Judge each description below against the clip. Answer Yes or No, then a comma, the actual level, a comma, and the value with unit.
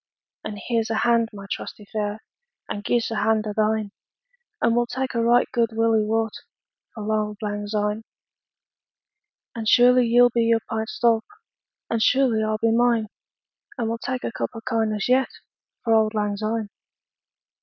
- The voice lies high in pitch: Yes, high, 225 Hz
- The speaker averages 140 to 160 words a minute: No, average, 175 wpm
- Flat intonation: Yes, narrow, 1.6 semitones